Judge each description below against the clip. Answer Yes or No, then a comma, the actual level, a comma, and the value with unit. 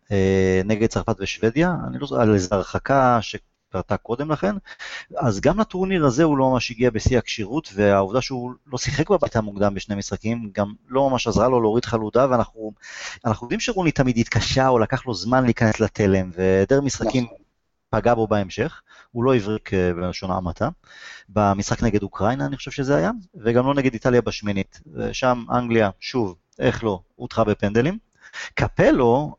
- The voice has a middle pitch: No, low, 115 Hz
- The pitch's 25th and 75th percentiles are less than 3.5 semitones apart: No, average, 4.3 semitones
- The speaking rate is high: Yes, fast, 155 wpm